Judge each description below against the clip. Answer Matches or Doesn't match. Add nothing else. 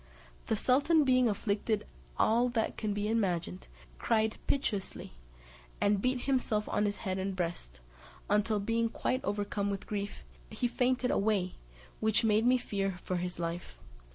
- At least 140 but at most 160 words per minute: Matches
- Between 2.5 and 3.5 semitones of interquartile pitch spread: Matches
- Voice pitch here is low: Doesn't match